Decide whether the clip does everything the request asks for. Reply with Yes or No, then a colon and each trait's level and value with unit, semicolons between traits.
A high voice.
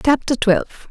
Yes: high, 240 Hz